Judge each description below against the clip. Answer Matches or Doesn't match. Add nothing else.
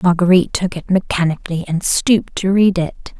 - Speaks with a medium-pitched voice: Matches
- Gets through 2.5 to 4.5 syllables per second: Doesn't match